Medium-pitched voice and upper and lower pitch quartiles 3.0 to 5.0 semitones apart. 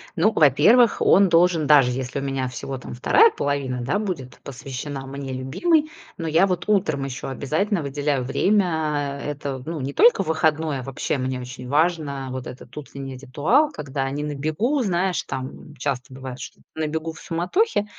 Yes: medium, 145 Hz; average, 4.5 semitones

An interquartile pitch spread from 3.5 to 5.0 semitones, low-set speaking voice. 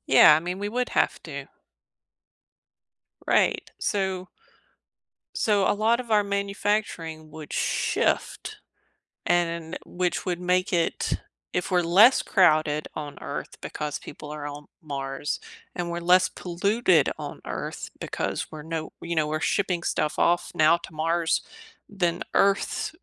No: average, 3.9 semitones; medium, 175 Hz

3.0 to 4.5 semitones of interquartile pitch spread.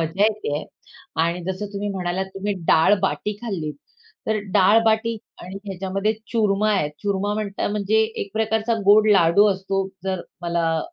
No: narrow, 2.4 semitones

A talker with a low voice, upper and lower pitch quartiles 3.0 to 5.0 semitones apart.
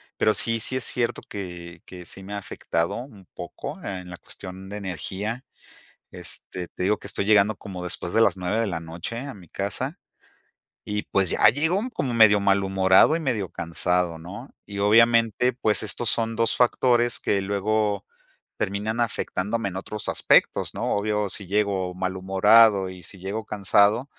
Yes: low, 100 Hz; average, 3.3 semitones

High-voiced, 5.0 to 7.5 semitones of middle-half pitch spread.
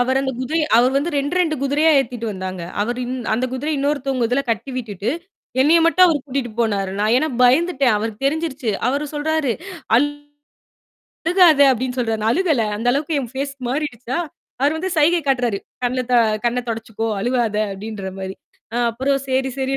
No: very high, 260 Hz; average, 4.2 semitones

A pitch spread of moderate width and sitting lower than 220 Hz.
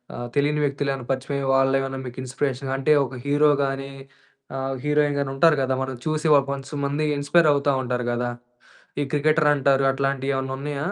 No: narrow, 1.6 semitones; medium, 140 Hz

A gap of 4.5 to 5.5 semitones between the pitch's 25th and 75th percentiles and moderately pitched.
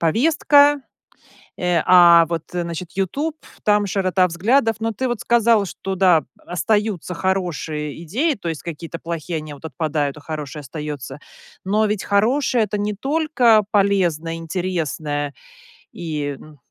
Yes: average, 5.1 semitones; medium, 180 Hz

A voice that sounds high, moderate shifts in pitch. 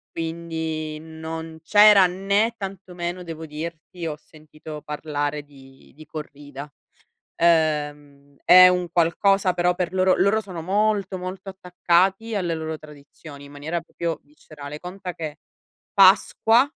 No: medium, 165 Hz; average, 3.4 semitones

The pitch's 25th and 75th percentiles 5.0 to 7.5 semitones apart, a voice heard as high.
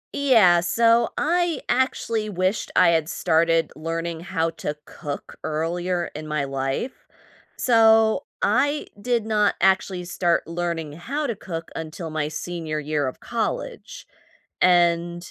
No: average, 5.3 semitones; medium, 175 Hz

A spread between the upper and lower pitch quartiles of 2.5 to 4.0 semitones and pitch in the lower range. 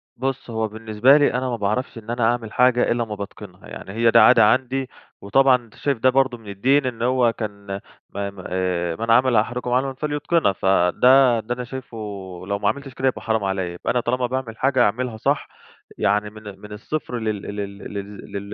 Yes: average, 3.7 semitones; low, 115 Hz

